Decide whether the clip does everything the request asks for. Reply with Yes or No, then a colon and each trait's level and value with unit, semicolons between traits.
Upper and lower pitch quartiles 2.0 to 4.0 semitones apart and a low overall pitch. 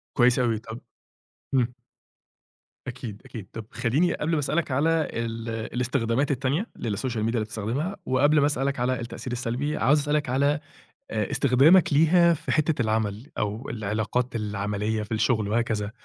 No: average, 4.6 semitones; low, 125 Hz